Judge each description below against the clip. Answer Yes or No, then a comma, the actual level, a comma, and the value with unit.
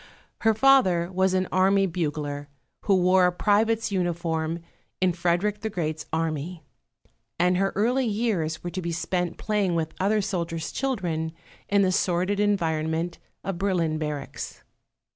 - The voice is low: No, medium, 180 Hz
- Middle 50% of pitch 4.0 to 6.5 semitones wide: No, average, 3.5 semitones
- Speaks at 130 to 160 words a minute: Yes, average, 140 wpm